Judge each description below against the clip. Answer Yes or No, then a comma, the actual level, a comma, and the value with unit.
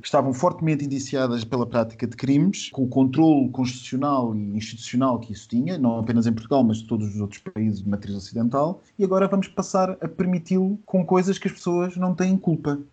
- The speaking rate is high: Yes, fast, 205 wpm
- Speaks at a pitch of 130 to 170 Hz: Yes, medium, 140 Hz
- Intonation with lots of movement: Yes, wide, 7.7 semitones